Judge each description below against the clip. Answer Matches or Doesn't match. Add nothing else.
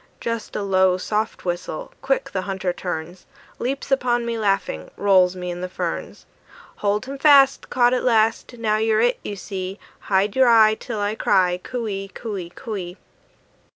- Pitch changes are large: Doesn't match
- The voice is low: Doesn't match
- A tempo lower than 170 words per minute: Doesn't match